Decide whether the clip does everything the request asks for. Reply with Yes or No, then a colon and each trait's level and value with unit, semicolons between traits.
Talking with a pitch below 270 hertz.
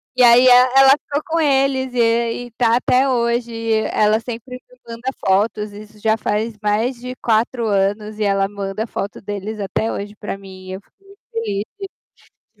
Yes: high, 230 Hz